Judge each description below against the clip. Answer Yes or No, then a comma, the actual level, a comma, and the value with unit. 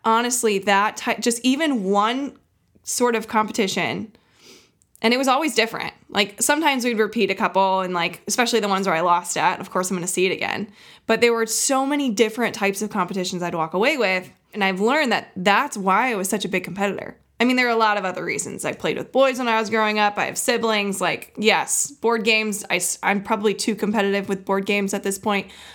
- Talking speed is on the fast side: Yes, fast, 225 wpm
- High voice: Yes, high, 210 Hz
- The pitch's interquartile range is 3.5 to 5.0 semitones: No, average, 3.0 semitones